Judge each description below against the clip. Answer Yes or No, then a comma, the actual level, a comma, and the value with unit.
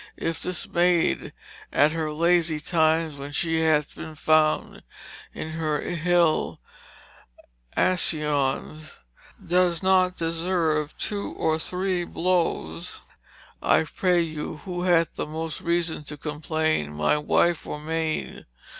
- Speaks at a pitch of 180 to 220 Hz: No, medium, 160 Hz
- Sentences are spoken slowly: Yes, slow, 120 wpm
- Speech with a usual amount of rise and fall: No, narrow, 2.2 semitones